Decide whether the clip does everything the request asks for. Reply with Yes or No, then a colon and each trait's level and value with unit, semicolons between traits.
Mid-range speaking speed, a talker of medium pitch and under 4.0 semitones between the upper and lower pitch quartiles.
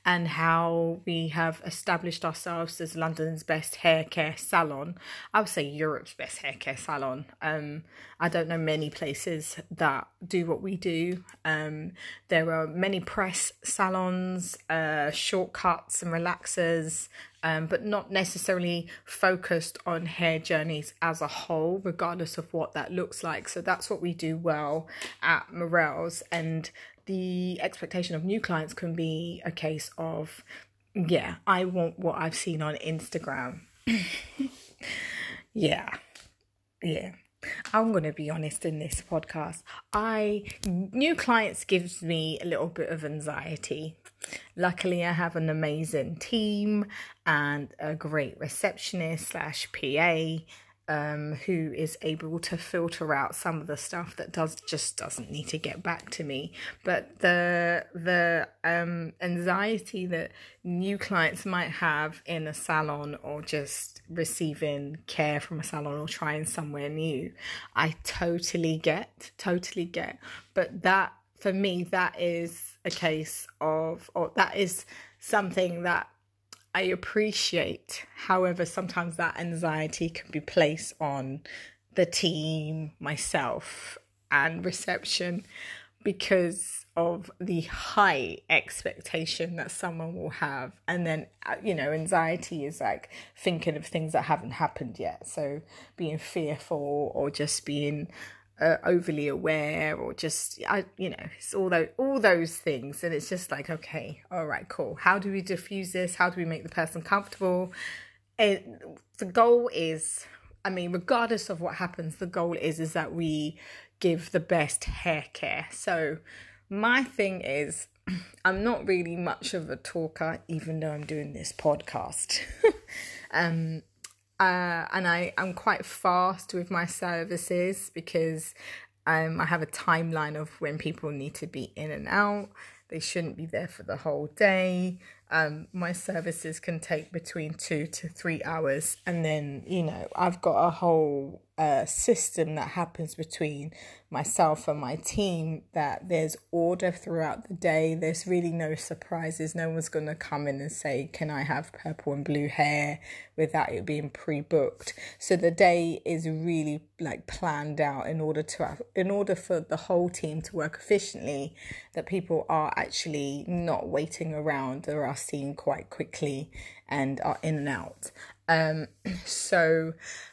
Yes: average, 150 wpm; medium, 165 Hz; narrow, 2.6 semitones